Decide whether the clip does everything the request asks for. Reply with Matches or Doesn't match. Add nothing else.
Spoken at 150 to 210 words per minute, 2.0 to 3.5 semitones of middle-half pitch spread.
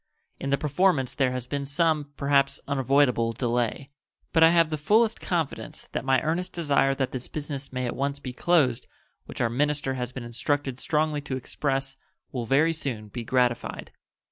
Matches